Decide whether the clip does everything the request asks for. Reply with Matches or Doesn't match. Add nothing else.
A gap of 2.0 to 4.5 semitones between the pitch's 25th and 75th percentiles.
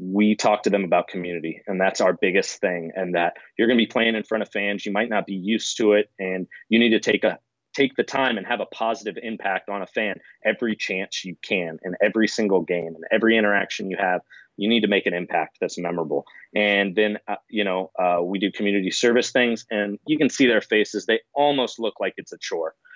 Matches